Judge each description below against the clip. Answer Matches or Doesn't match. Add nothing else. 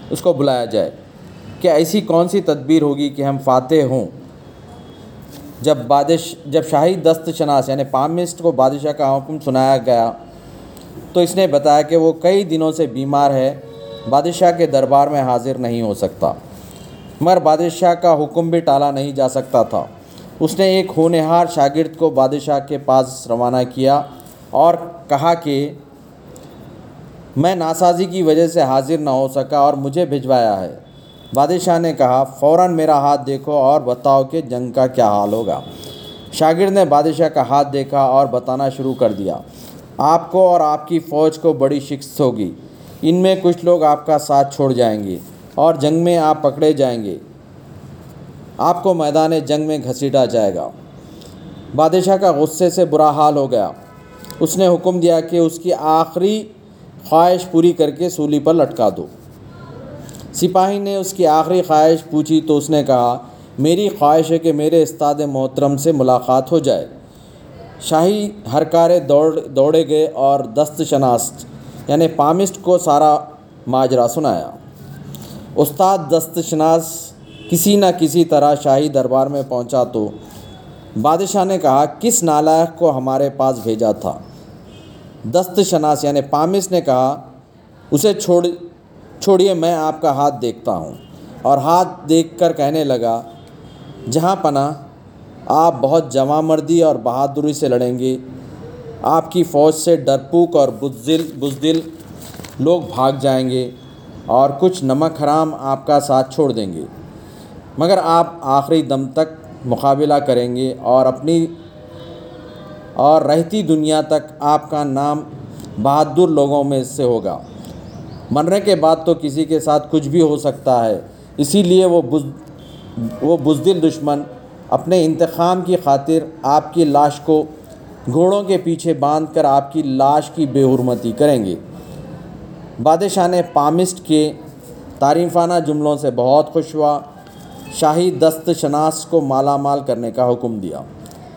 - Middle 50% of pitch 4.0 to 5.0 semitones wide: Doesn't match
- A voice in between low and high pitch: Matches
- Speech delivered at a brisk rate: Matches